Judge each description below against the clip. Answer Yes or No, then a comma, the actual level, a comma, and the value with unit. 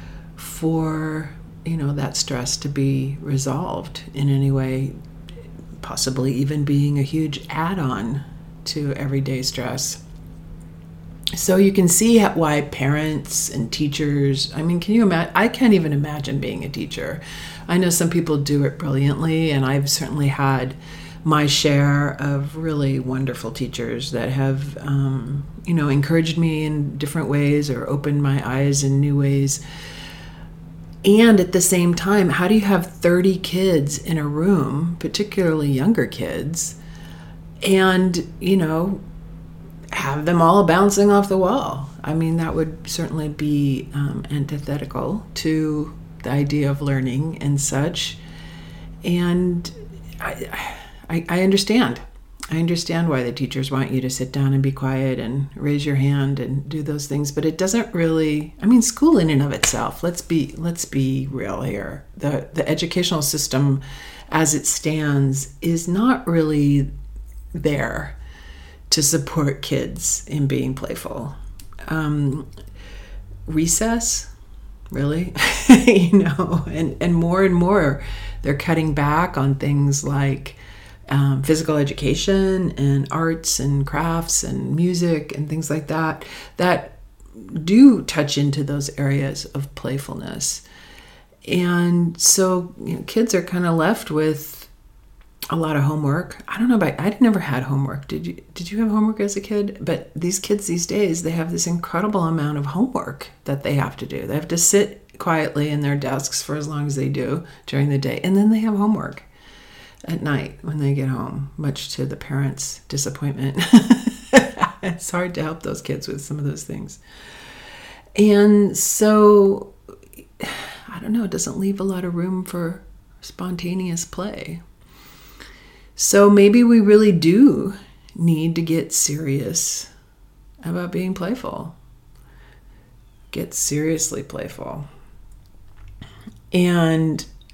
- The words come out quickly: No, average, 145 wpm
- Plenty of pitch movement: No, average, 4.2 semitones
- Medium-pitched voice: Yes, medium, 150 Hz